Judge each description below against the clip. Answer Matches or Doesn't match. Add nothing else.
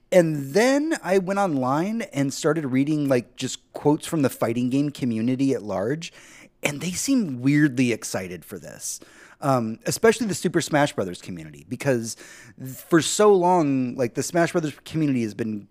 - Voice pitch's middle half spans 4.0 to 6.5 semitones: Matches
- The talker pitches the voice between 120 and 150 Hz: Matches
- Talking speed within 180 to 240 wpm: Doesn't match